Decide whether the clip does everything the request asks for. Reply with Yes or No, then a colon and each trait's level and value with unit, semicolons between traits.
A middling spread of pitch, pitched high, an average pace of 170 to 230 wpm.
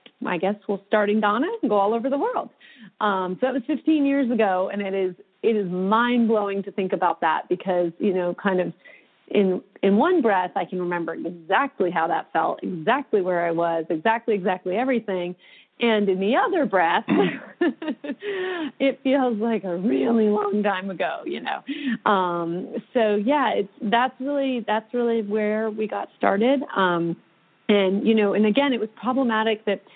Yes: average, 4.6 semitones; high, 215 Hz; average, 180 wpm